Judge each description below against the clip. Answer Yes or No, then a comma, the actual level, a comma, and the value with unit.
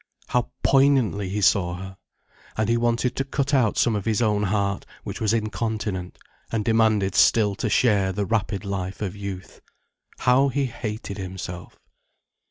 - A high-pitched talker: No, low, 105 Hz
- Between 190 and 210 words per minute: No, average, 160 wpm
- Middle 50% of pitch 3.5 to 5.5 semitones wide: No, average, 3.0 semitones